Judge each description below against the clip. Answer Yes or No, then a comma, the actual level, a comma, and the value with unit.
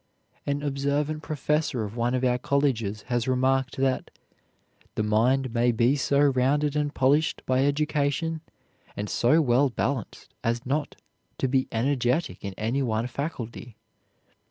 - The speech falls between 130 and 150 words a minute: Yes, average, 140 wpm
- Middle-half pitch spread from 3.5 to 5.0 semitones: No, average, 3.1 semitones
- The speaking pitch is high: No, low, 130 Hz